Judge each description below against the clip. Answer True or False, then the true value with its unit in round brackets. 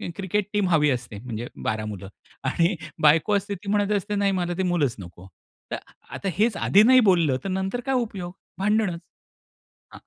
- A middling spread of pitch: False (5.8 semitones)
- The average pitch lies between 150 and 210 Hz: True (185 Hz)